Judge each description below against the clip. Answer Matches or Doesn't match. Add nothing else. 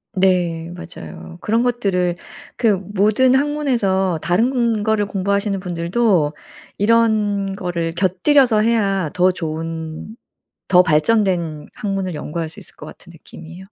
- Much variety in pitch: Doesn't match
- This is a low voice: Doesn't match